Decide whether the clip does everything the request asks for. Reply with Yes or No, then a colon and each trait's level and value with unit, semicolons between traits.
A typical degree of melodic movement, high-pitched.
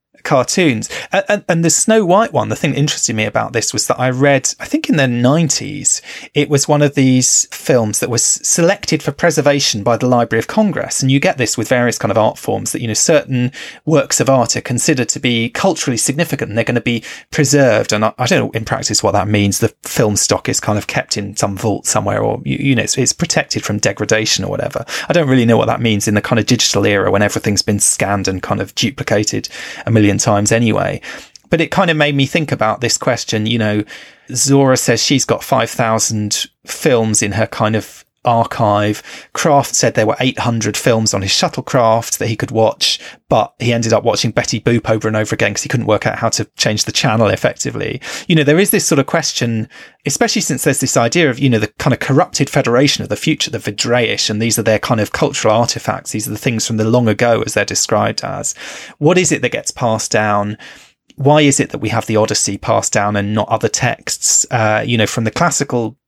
No: average, 4.5 semitones; low, 120 Hz